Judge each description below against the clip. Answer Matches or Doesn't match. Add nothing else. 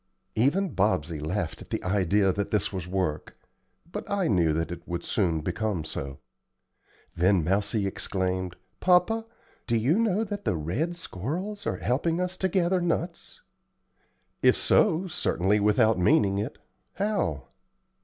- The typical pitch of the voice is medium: Doesn't match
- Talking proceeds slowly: Doesn't match